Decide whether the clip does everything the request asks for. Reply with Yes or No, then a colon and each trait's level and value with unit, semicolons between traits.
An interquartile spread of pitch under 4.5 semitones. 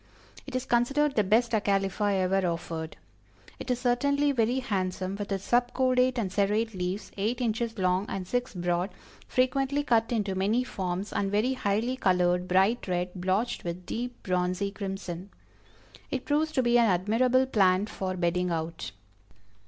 No: average, 4.9 semitones